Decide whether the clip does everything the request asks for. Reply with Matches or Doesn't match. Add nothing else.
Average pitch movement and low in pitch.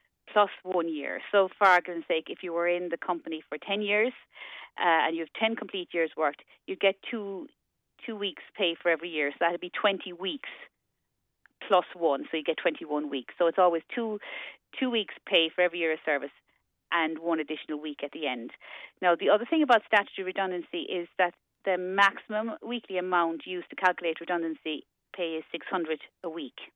Doesn't match